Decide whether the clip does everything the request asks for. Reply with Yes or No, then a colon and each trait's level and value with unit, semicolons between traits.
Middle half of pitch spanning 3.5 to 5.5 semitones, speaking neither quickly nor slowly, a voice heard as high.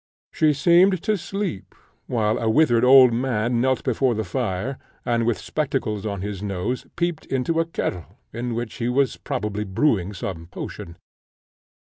No: average, 4.7 semitones; average, 155 wpm; low, 120 Hz